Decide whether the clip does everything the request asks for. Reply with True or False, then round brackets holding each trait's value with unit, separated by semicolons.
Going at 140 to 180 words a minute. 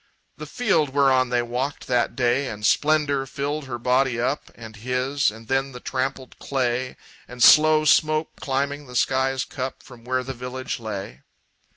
True (165 wpm)